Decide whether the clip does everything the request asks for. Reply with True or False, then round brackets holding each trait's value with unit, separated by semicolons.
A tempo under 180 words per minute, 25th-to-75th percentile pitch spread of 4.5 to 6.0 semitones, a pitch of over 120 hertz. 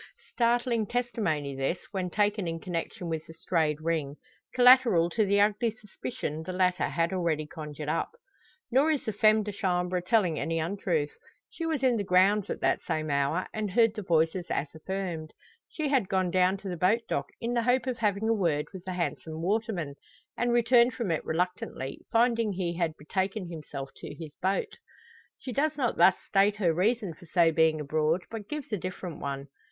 False (190 wpm; 5.3 semitones; 185 Hz)